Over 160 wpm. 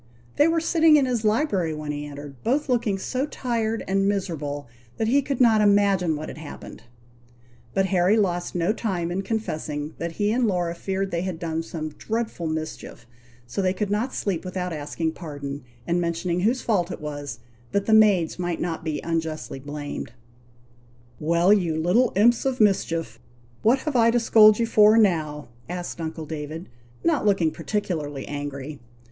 Yes: average, 175 wpm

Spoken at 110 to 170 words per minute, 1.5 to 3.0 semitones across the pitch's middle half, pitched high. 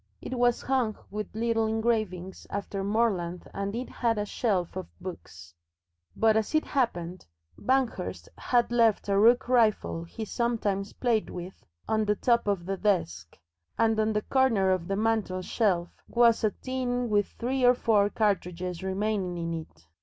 No: average, 160 wpm; average, 3.9 semitones; high, 210 Hz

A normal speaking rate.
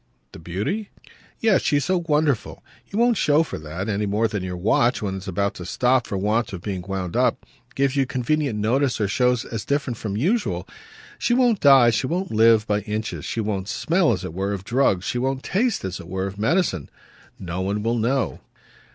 No: fast, 210 wpm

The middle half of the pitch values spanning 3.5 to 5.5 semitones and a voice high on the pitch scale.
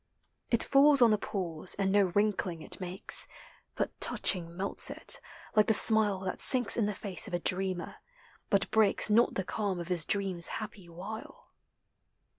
No: average, 3.0 semitones; high, 195 Hz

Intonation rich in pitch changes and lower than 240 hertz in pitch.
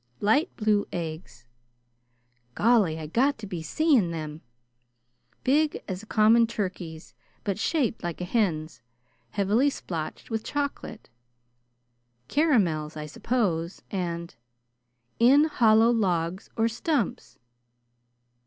Yes: wide, 6.8 semitones; medium, 185 Hz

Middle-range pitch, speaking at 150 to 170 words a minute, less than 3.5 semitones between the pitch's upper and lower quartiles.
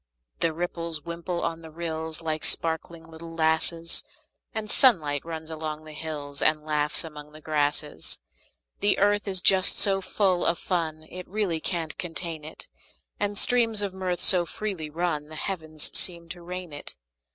Yes: medium, 165 Hz; average, 165 wpm; narrow, 2.6 semitones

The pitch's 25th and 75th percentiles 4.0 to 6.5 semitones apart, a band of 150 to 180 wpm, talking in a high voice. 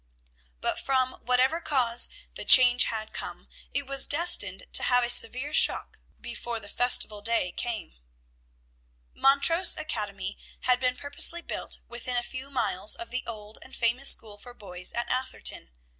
No: average, 3.3 semitones; average, 155 wpm; high, 245 Hz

